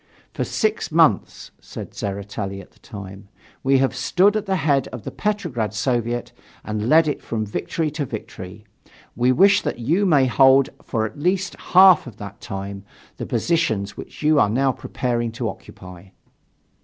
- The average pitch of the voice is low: Yes, low, 125 Hz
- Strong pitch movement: Yes, wide, 7.3 semitones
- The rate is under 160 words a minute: No, average, 170 wpm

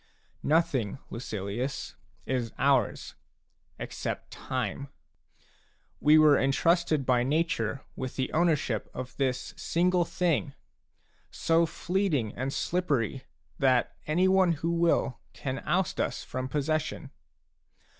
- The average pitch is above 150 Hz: No, medium, 140 Hz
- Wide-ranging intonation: No, average, 4.5 semitones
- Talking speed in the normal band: No, slow, 105 wpm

